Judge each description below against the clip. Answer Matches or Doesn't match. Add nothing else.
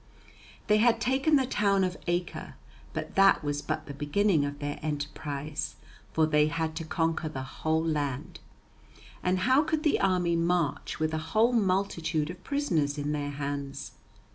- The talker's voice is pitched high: Doesn't match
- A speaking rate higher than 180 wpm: Doesn't match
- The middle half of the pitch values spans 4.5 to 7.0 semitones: Matches